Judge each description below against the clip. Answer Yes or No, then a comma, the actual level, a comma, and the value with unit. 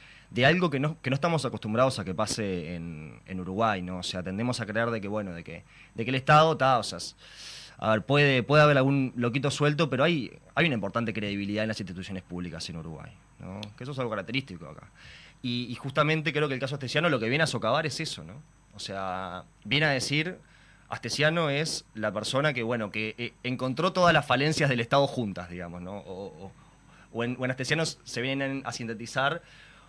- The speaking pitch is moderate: No, low, 125 Hz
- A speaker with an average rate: No, fast, 220 wpm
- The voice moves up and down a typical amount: No, wide, 5.8 semitones